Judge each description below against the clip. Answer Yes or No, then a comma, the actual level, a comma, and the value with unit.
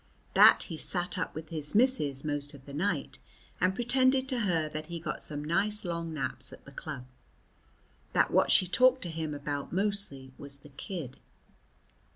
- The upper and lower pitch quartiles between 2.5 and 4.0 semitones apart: No, average, 5.3 semitones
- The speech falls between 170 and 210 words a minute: Yes, average, 180 wpm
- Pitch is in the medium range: Yes, medium, 165 Hz